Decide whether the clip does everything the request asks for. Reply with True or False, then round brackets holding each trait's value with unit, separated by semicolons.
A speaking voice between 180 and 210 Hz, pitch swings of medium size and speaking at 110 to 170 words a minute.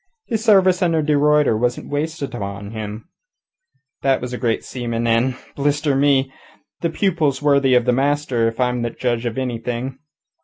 False (130 Hz; 3.8 semitones; 165 wpm)